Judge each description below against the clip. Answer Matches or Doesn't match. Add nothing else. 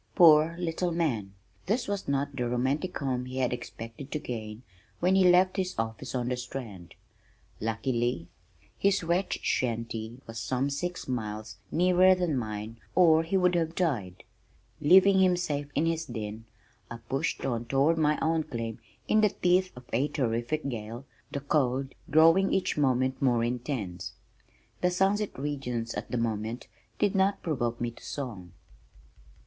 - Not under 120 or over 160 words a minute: Matches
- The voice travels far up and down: Matches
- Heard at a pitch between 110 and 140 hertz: Matches